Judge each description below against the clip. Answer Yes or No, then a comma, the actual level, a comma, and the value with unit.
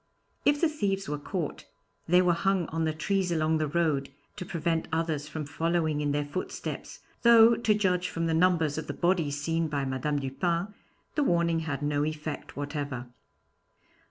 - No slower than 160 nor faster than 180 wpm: Yes, average, 175 wpm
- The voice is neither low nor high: Yes, medium, 165 Hz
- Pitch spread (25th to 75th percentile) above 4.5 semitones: No, average, 3.5 semitones